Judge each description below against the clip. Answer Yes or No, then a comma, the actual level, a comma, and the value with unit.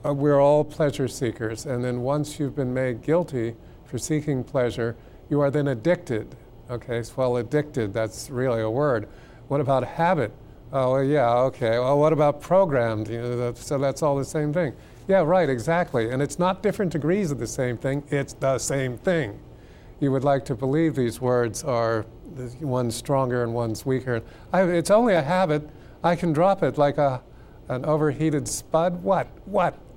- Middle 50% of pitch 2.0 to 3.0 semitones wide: No, average, 3.7 semitones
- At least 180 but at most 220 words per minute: Yes, average, 195 wpm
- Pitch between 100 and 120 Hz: No, low, 135 Hz